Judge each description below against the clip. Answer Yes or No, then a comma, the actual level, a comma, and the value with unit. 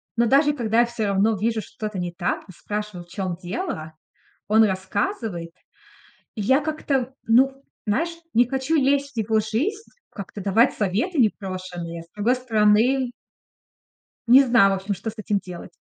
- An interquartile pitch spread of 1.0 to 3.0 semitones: No, average, 5.1 semitones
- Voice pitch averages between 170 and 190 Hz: No, high, 220 Hz